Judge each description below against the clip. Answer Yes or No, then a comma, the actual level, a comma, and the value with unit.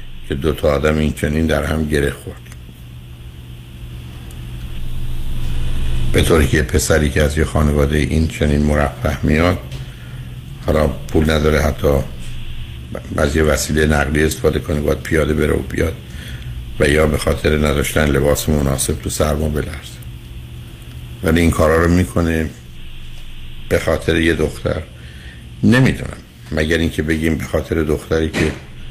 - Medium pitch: No, very low, 75 Hz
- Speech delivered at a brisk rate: No, average, 130 wpm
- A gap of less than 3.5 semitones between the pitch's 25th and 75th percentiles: No, average, 4.0 semitones